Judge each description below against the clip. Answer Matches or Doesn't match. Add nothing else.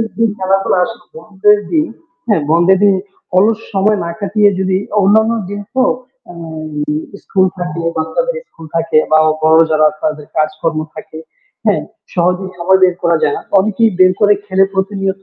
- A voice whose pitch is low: Doesn't match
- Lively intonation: Doesn't match